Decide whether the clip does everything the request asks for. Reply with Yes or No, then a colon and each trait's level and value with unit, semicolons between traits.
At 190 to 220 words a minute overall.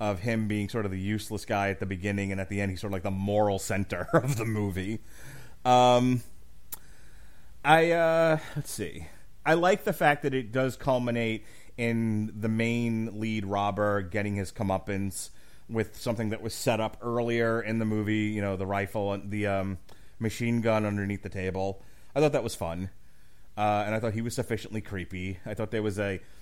Yes: average, 195 wpm